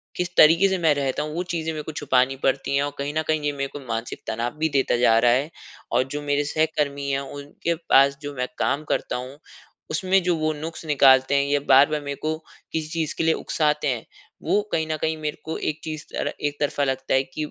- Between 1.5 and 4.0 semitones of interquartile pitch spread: Yes, narrow, 2.4 semitones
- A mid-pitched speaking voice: Yes, medium, 145 Hz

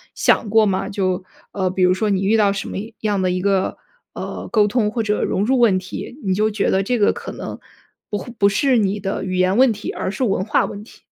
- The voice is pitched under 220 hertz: Yes, high, 205 Hz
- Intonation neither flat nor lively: No, narrow, 2.3 semitones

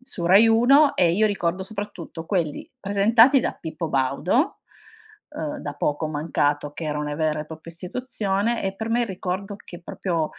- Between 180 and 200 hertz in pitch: Yes, medium, 185 Hz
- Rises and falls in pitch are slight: No, wide, 5.8 semitones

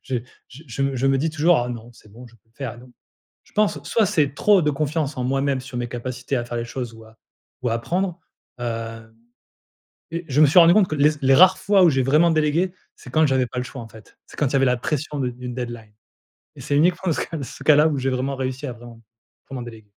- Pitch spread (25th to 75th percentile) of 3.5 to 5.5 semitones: Yes, average, 4.1 semitones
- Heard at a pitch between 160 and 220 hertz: No, low, 135 Hz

